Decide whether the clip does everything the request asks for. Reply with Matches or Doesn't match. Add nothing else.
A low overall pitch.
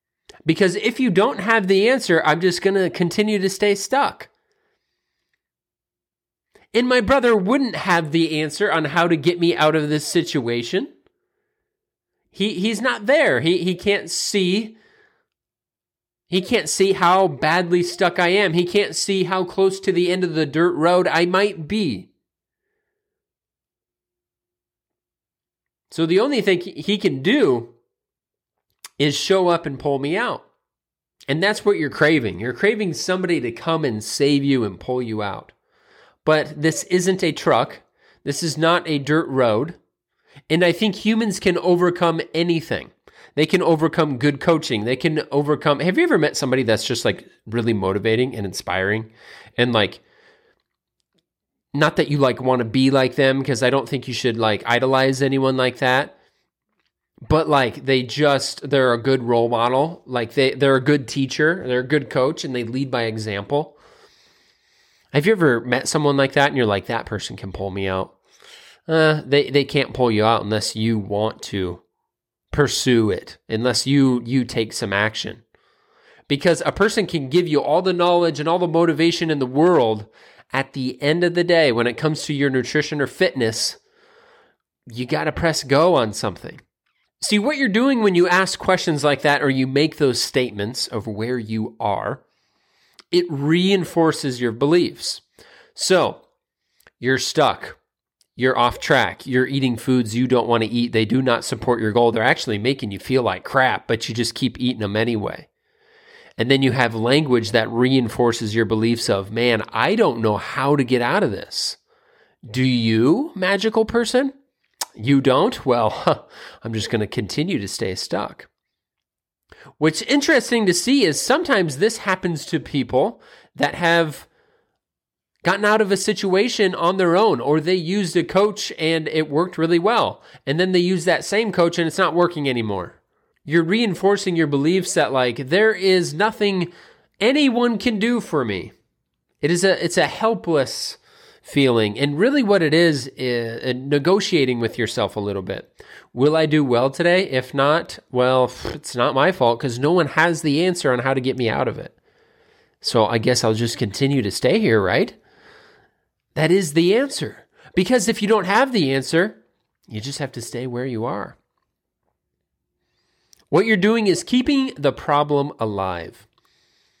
Doesn't match